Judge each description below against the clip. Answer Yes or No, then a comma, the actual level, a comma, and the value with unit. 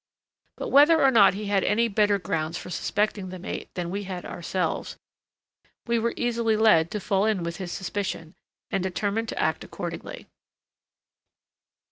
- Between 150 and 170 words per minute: Yes, average, 160 wpm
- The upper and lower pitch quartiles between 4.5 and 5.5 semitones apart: No, average, 3.5 semitones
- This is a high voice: Yes, high, 200 Hz